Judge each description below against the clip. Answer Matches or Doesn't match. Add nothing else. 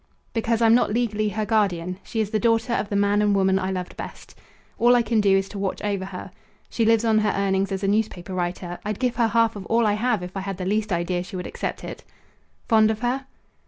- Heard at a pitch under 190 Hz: Doesn't match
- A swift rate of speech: Matches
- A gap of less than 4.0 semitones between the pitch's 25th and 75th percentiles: Matches